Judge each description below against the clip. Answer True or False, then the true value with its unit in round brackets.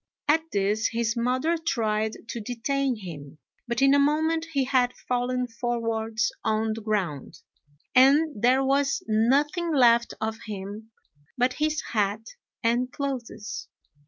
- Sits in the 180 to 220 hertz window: False (240 Hz)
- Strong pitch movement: False (3.9 semitones)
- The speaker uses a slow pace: True (130 wpm)